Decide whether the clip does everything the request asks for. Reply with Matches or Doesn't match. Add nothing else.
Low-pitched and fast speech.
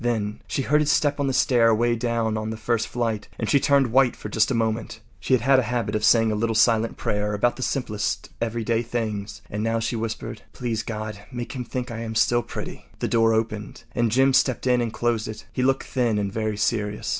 Matches